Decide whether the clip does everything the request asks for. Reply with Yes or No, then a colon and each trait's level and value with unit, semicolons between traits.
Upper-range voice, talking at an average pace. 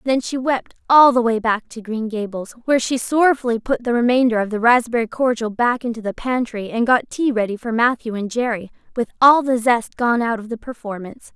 No: high, 235 Hz; fast, 215 wpm